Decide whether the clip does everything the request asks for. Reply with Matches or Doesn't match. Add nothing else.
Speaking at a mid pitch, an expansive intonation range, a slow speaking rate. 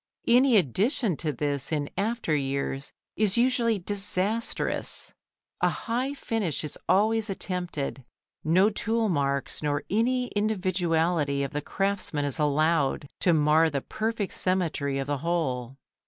Matches